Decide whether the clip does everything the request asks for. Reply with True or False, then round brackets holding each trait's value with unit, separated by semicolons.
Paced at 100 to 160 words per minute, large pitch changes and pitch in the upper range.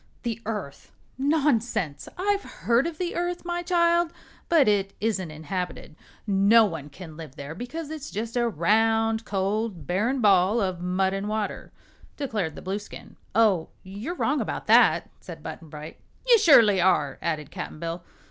True (155 wpm; 6.5 semitones; 210 Hz)